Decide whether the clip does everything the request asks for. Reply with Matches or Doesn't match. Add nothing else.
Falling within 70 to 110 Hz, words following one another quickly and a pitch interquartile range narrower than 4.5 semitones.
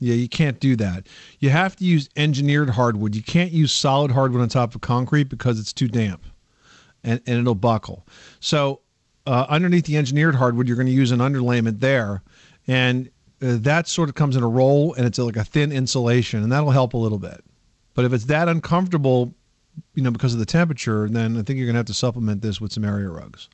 Doesn't match